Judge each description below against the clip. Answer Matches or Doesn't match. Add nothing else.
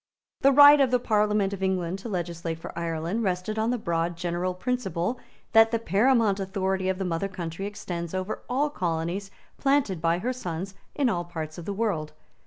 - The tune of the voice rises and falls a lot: Doesn't match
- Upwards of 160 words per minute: Matches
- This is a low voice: Doesn't match